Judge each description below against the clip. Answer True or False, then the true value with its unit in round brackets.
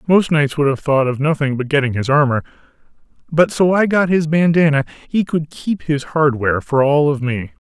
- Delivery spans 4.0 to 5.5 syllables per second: True (5.3 syllables/s)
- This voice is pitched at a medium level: True (150 Hz)